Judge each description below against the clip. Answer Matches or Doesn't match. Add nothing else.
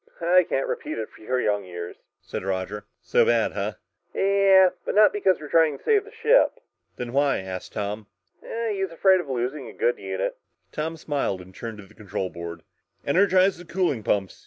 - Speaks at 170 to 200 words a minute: Matches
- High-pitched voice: Doesn't match